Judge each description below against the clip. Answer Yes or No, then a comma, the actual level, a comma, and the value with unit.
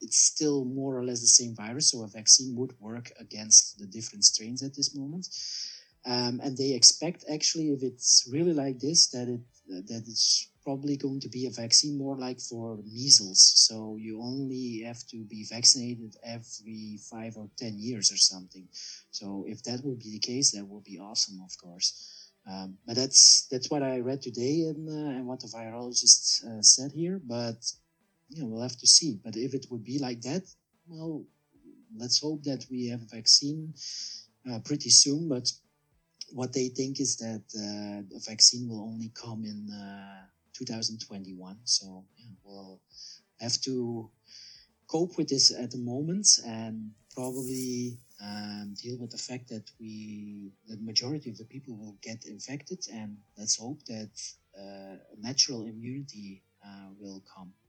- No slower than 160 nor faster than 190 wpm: Yes, fast, 170 wpm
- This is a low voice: Yes, low, 120 Hz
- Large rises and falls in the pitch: No, average, 3.7 semitones